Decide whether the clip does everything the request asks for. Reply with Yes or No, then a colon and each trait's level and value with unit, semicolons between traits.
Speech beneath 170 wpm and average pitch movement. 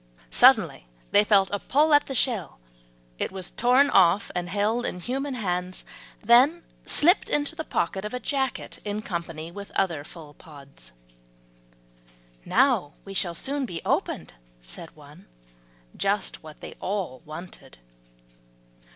No: average, 140 wpm; wide, 6.7 semitones